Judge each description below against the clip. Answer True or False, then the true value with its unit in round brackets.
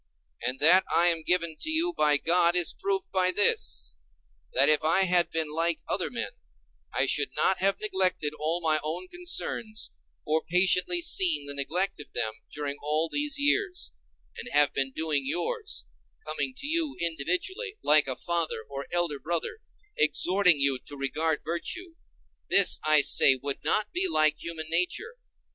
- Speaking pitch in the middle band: True (170 Hz)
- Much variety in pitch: False (4.7 semitones)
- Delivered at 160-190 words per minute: True (165 wpm)